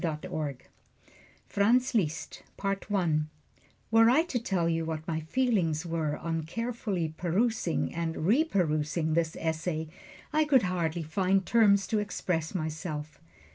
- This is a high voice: No, medium, 170 Hz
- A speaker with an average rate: No, slow, 130 wpm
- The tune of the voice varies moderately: Yes, average, 4.6 semitones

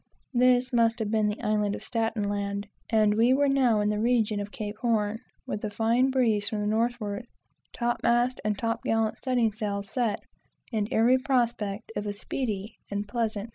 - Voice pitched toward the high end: Yes, high, 220 Hz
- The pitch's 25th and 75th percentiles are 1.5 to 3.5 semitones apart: Yes, narrow, 2.5 semitones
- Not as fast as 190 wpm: No, average, 195 wpm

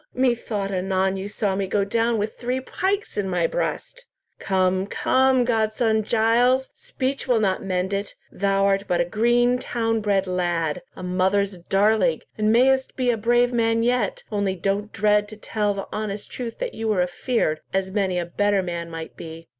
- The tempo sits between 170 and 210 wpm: Yes, average, 180 wpm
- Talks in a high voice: Yes, high, 205 Hz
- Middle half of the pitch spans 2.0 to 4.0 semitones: Yes, average, 3.7 semitones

